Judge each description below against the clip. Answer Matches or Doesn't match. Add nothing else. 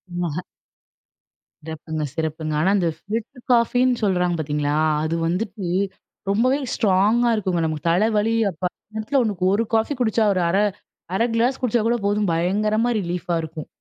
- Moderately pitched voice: Doesn't match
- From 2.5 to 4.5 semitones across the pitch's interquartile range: Doesn't match